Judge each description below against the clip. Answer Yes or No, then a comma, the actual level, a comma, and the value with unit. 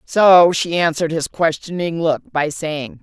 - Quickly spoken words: No, average, 160 wpm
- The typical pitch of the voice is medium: Yes, medium, 165 Hz